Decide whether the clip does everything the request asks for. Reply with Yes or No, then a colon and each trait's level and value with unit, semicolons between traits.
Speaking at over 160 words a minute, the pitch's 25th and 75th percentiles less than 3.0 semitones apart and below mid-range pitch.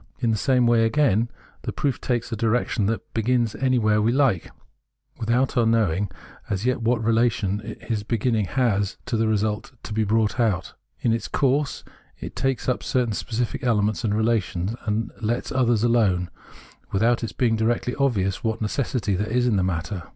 Yes: average, 185 wpm; narrow, 2.5 semitones; low, 115 Hz